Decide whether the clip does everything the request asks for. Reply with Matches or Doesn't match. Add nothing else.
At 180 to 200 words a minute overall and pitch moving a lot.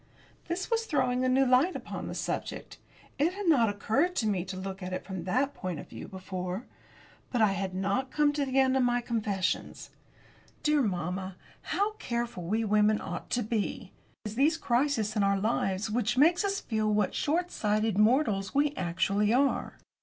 Matches